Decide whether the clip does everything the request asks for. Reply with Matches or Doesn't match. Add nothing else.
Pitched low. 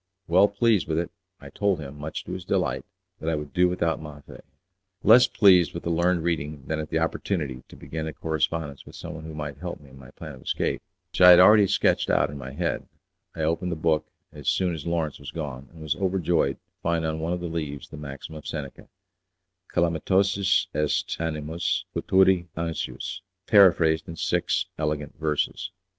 Matches